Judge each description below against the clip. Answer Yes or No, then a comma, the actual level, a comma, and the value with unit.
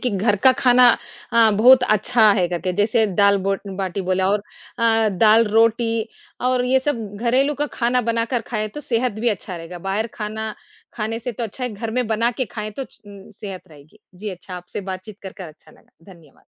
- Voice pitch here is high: Yes, high, 220 Hz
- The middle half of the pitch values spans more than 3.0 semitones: Yes, average, 3.5 semitones